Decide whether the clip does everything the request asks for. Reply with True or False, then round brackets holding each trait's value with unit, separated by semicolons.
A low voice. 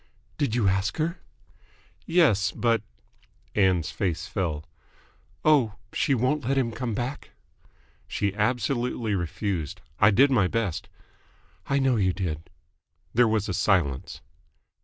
True (110 Hz)